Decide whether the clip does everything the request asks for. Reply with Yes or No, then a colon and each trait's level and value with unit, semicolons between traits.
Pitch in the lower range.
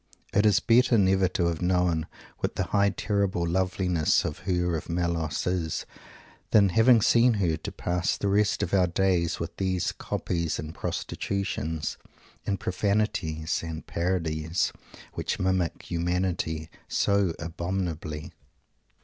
Yes: very low, 90 Hz